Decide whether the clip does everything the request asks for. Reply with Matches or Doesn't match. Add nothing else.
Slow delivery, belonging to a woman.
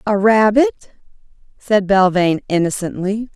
Matches